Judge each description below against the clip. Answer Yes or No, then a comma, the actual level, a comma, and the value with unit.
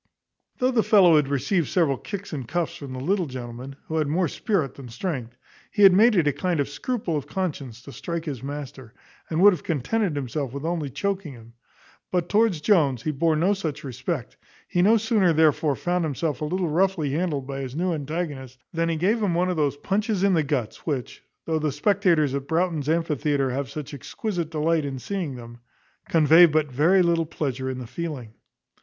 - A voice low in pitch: No, medium, 155 Hz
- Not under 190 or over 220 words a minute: Yes, average, 200 wpm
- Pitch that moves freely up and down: No, average, 4.6 semitones